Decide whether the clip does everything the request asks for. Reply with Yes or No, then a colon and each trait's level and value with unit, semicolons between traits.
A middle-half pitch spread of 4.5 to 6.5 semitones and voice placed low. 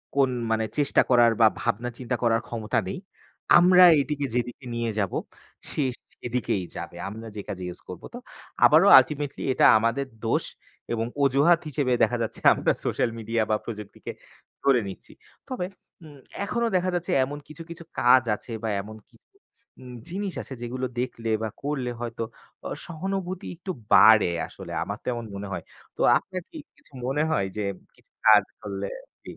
Yes: average, 5.2 semitones; low, 125 Hz